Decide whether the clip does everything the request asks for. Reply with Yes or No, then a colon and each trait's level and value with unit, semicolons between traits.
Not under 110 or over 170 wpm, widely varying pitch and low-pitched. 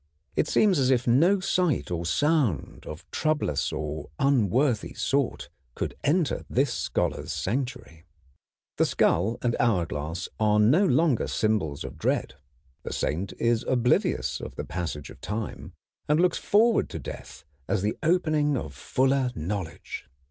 Yes: average, 140 wpm; wide, 8.5 semitones; low, 120 Hz